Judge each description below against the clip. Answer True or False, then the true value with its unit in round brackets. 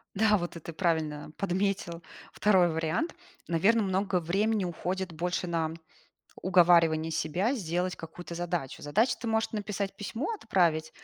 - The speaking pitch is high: False (180 Hz)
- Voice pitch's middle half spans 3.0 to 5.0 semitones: True (3.4 semitones)